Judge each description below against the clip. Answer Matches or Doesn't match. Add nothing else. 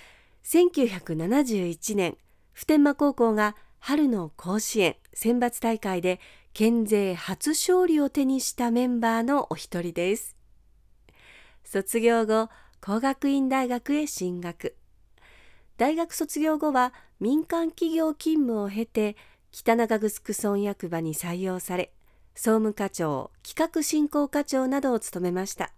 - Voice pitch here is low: Doesn't match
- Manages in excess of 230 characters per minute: Doesn't match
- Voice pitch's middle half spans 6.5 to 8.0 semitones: Matches